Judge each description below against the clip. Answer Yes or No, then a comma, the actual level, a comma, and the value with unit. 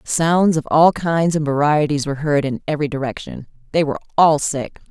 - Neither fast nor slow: Yes, average, 185 wpm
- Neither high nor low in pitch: Yes, medium, 150 Hz